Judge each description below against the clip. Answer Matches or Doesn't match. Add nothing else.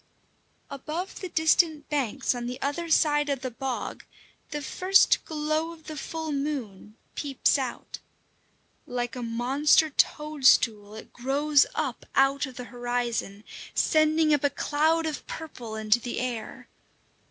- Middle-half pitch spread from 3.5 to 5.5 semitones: Matches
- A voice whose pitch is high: Matches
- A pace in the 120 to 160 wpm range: Matches